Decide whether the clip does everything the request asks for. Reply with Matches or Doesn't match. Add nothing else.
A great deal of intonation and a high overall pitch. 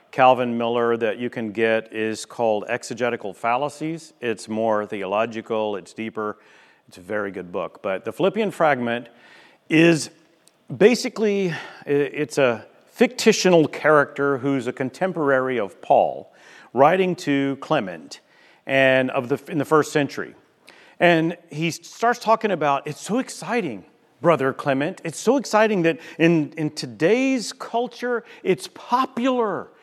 Doesn't match